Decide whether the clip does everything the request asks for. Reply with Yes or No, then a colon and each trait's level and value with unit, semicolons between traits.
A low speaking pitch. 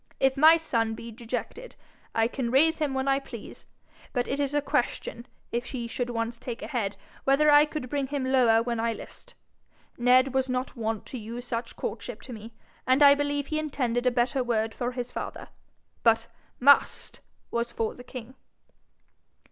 No: very high, 250 Hz